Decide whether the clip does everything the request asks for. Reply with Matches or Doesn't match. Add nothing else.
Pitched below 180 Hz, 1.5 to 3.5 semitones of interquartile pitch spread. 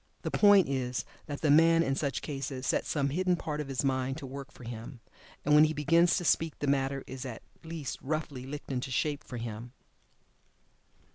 Matches